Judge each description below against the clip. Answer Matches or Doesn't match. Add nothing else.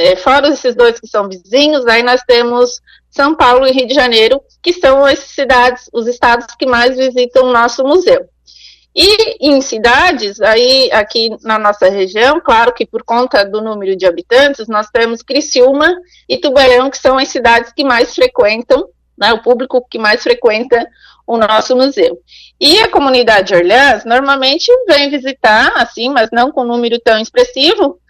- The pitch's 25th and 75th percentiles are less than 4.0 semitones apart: Matches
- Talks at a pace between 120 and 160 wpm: Doesn't match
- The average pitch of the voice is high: Matches